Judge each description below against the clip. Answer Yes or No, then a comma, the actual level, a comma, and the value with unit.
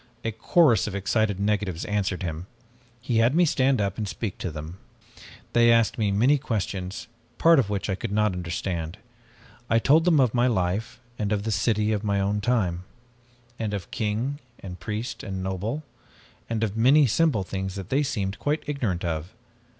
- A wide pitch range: No, average, 3.8 semitones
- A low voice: Yes, low, 105 Hz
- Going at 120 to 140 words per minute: No, average, 180 wpm